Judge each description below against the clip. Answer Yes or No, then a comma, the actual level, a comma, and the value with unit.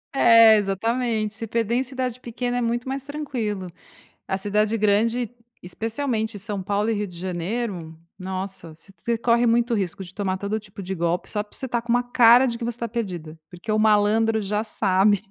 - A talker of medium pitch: No, high, 215 Hz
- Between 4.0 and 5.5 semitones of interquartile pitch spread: No, average, 3.3 semitones